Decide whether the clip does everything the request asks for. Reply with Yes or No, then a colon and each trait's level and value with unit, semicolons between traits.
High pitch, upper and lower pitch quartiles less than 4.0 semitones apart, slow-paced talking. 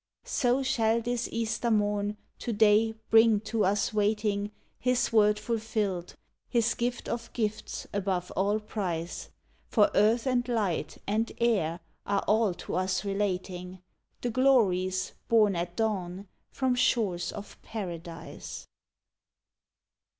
Yes: high, 210 Hz; average, 3.3 semitones; slow, 120 wpm